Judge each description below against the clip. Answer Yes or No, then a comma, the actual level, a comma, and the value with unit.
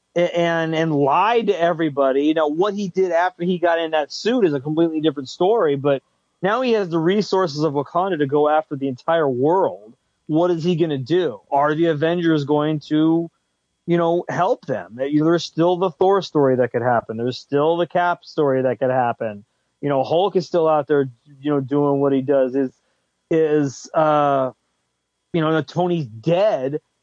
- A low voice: No, medium, 155 Hz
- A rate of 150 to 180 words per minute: No, average, 195 wpm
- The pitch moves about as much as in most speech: Yes, average, 3.7 semitones